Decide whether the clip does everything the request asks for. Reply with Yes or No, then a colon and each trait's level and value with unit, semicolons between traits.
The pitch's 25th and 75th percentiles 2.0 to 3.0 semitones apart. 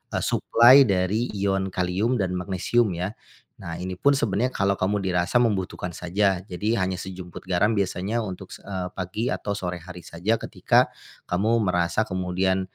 Yes: average, 2.7 semitones